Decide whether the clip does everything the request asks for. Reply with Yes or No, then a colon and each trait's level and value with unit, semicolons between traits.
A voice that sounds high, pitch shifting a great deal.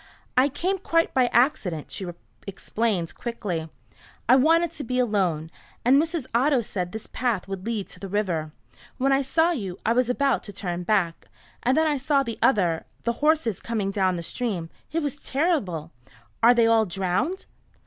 Yes: high, 230 Hz; wide, 6.6 semitones